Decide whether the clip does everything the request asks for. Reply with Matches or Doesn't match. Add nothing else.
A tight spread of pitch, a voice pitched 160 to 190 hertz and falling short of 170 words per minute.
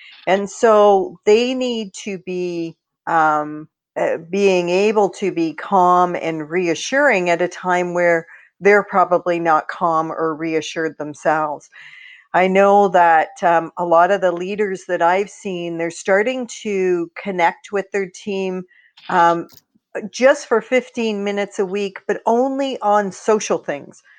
Doesn't match